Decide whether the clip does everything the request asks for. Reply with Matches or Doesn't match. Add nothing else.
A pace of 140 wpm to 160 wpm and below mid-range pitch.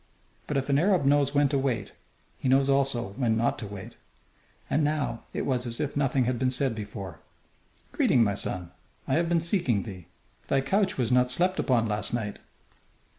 Doesn't match